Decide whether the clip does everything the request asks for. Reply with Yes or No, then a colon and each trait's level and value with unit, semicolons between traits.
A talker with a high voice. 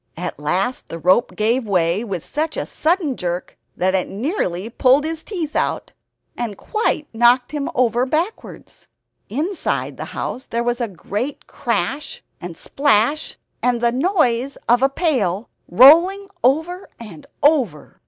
Yes: high, 245 Hz